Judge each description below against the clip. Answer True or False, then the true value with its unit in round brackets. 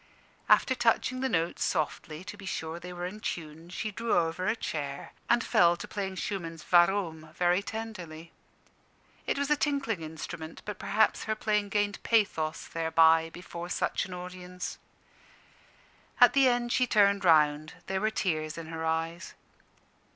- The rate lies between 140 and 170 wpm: True (160 wpm)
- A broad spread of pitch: False (4.5 semitones)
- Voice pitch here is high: False (180 Hz)